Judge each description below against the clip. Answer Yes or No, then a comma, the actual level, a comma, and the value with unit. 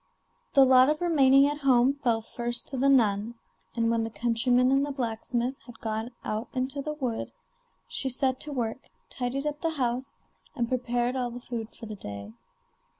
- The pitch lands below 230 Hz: No, very high, 250 Hz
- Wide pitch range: No, average, 2.7 semitones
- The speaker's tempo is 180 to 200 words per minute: Yes, average, 185 wpm